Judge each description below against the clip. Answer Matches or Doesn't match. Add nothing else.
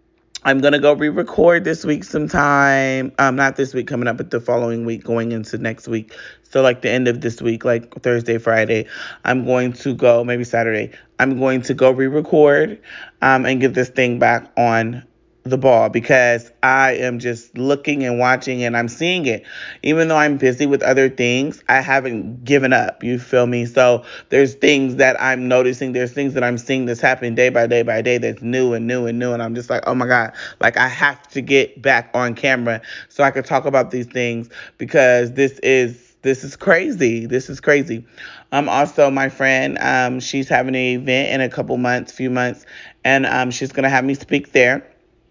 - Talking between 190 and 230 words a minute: Matches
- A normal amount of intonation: Doesn't match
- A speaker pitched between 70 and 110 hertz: Doesn't match